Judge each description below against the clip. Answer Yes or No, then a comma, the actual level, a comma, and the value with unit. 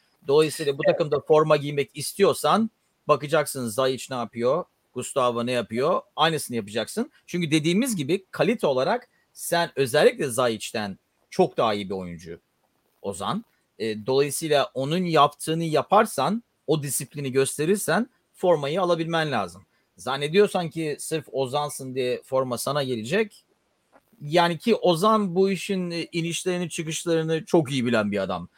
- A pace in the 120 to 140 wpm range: Yes, average, 125 wpm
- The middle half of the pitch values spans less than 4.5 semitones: No, average, 5.0 semitones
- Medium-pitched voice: Yes, medium, 150 Hz